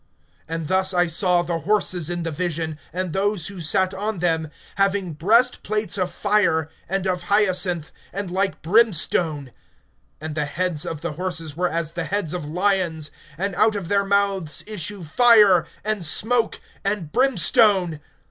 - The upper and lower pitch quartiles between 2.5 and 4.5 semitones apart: Yes, average, 3.6 semitones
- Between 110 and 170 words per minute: Yes, average, 155 wpm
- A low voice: No, medium, 180 Hz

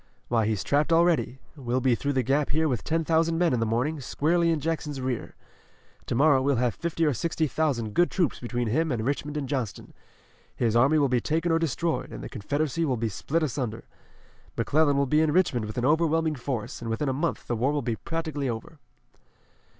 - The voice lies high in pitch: No, medium, 140 Hz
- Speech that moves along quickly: Yes, fast, 210 wpm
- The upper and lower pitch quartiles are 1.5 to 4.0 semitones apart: No, average, 4.6 semitones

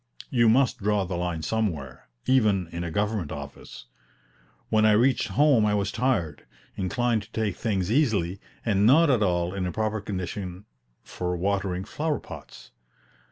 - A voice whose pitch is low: Yes, low, 100 Hz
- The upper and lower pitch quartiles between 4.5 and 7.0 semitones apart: No, average, 3.9 semitones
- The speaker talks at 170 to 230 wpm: No, average, 160 wpm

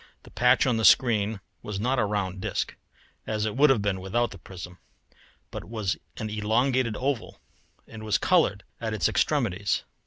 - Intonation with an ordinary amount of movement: Yes, average, 3.2 semitones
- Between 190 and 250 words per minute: No, average, 175 wpm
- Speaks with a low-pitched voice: Yes, low, 110 Hz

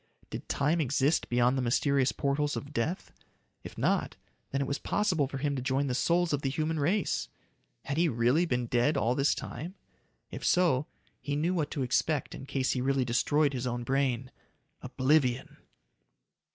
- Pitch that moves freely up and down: No, average, 3.1 semitones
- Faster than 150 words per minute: Yes, average, 180 wpm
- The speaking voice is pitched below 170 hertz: Yes, medium, 140 Hz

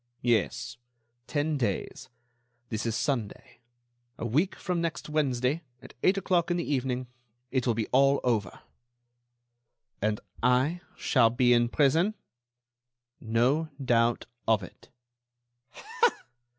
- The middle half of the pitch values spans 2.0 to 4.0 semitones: No, average, 4.5 semitones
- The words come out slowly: Yes, slow, 115 wpm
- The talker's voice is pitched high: No, low, 125 Hz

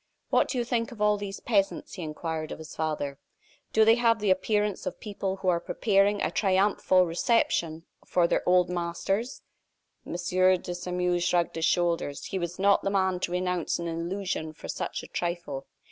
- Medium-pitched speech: Yes, medium, 180 Hz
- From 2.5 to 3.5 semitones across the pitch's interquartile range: Yes, average, 2.8 semitones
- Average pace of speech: Yes, average, 185 wpm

